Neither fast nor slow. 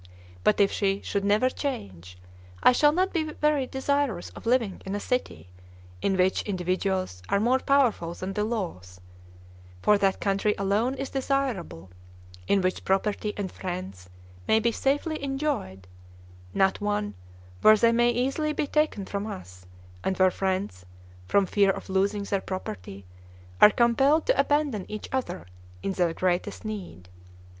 Yes: average, 150 wpm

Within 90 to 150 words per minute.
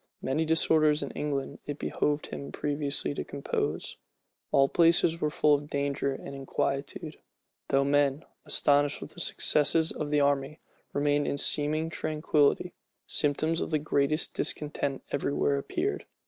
Yes: average, 145 wpm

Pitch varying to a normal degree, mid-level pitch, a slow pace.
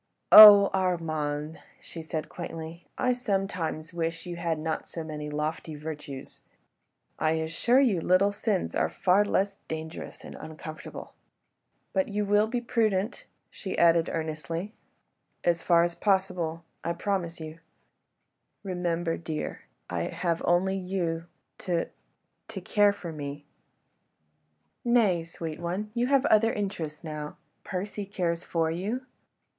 Yes: average, 3.8 semitones; medium, 170 Hz; slow, 130 wpm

